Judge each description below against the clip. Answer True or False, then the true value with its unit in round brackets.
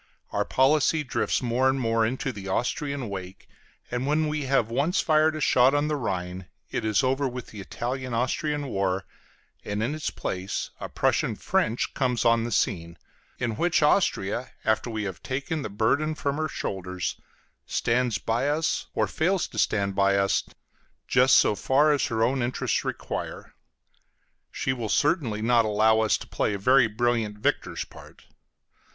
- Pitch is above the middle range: False (120 Hz)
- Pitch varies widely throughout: False (4.8 semitones)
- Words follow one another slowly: False (170 wpm)